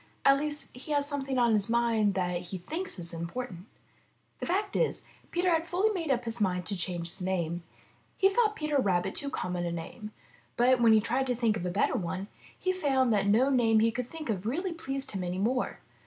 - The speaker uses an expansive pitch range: Yes, wide, 7.2 semitones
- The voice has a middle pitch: No, high, 235 Hz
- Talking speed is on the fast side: Yes, fast, 225 wpm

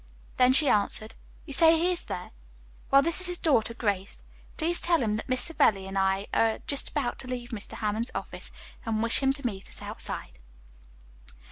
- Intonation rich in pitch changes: Yes, wide, 5.7 semitones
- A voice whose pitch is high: Yes, high, 245 Hz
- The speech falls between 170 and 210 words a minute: Yes, average, 195 wpm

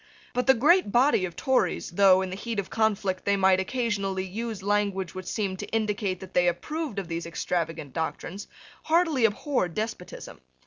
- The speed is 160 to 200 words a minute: Yes, average, 175 wpm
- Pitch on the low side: No, high, 200 Hz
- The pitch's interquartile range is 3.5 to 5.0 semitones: Yes, average, 3.8 semitones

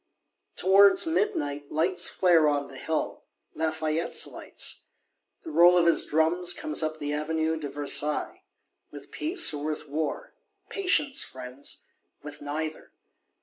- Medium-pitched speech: Yes, medium, 160 Hz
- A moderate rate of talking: No, slow, 130 wpm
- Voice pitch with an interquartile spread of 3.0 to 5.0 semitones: Yes, average, 3.5 semitones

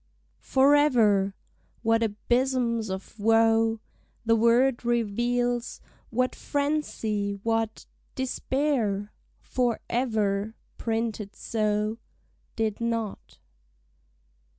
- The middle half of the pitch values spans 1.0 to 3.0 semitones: Yes, narrow, 2.4 semitones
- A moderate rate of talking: No, slow, 75 wpm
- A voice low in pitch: No, high, 225 Hz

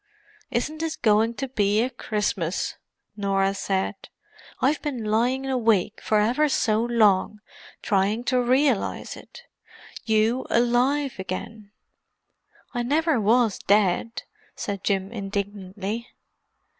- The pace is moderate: No, slow, 110 wpm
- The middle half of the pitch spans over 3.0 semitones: Yes, average, 3.6 semitones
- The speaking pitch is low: No, high, 220 Hz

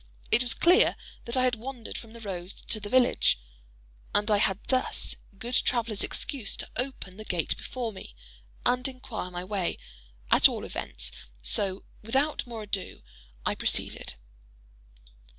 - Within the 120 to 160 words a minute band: Yes, average, 150 wpm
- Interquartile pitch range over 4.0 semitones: Yes, average, 4.5 semitones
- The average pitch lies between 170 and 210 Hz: No, high, 225 Hz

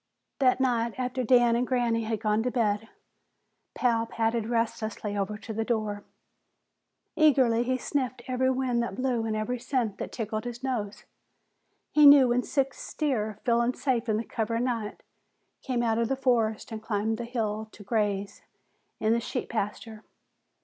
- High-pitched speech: Yes, high, 235 Hz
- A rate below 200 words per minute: Yes, average, 170 wpm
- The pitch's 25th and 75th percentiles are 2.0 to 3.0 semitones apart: Yes, narrow, 2.5 semitones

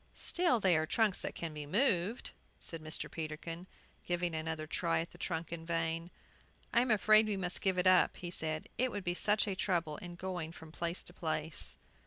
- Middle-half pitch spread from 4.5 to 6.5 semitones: No, average, 2.9 semitones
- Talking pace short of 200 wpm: No, fast, 205 wpm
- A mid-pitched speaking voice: Yes, medium, 175 Hz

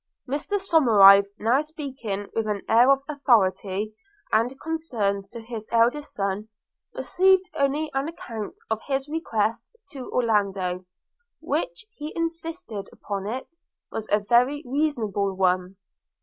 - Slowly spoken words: Yes, slow, 125 wpm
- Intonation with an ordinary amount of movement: No, wide, 6.4 semitones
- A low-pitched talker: No, high, 235 Hz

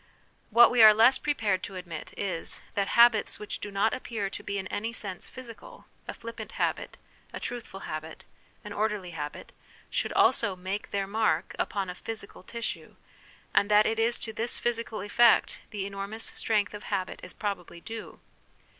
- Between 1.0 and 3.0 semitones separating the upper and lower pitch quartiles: Yes, average, 2.7 semitones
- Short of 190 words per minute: Yes, average, 175 wpm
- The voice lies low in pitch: No, high, 210 Hz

